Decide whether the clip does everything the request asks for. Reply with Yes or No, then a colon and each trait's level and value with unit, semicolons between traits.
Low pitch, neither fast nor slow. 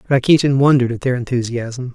Yes: low, 125 Hz; average, 155 wpm